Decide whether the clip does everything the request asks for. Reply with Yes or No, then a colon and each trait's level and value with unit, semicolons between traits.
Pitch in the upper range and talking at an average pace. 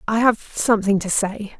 Yes: high, 210 Hz; average, 190 wpm